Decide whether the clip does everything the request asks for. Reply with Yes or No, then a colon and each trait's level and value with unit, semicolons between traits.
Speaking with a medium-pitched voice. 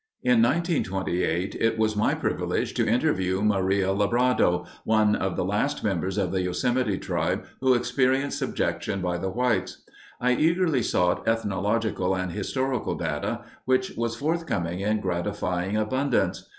No: low, 105 Hz